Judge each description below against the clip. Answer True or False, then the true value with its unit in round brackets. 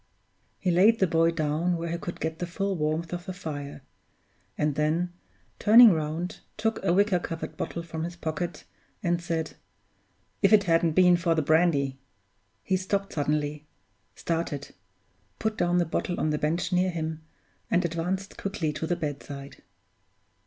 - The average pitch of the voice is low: False (170 Hz)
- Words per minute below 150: False (165 wpm)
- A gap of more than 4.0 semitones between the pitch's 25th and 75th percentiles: False (2.6 semitones)